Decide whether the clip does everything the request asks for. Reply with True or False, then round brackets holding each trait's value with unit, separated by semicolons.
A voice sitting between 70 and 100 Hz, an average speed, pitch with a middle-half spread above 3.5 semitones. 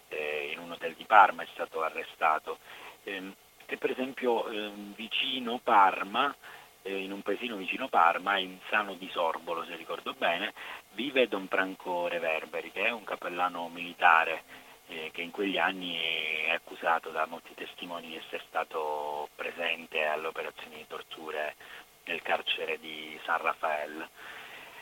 True (85 Hz; 145 wpm; 4.0 semitones)